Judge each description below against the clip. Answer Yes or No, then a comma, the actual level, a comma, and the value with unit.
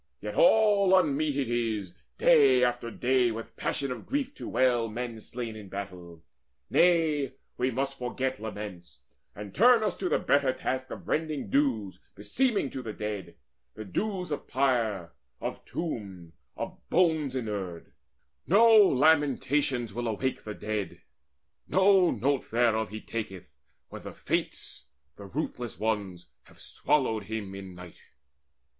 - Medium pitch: No, low, 125 Hz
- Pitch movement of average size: No, wide, 5.8 semitones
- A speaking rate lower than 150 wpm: Yes, average, 140 wpm